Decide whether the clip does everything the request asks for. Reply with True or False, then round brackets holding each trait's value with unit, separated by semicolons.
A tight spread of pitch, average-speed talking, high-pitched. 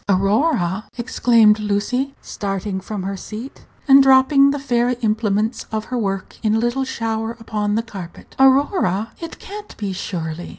False (4.6 semitones; 155 wpm; 220 Hz)